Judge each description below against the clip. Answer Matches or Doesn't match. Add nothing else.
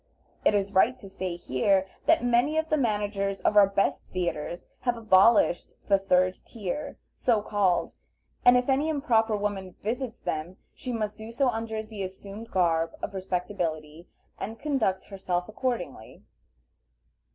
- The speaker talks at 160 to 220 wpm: Doesn't match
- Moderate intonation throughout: Matches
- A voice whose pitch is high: Matches